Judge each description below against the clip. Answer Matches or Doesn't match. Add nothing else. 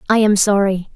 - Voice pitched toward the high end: Matches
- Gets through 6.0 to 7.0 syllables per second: Doesn't match